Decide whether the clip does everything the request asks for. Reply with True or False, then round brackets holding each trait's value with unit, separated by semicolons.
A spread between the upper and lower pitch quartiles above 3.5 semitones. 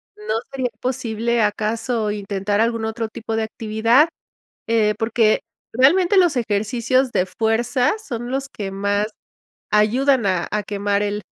False (2.9 semitones)